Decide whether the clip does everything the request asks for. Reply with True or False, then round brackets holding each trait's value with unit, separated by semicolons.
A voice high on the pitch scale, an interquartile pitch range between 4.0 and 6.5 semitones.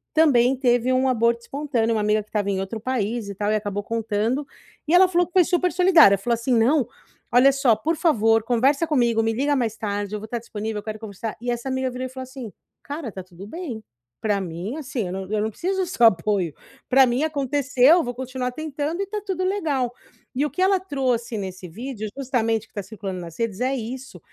True (240 Hz; 4.6 semitones)